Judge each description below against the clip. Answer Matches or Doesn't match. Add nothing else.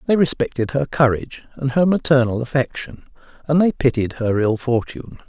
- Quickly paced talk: Doesn't match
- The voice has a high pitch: Doesn't match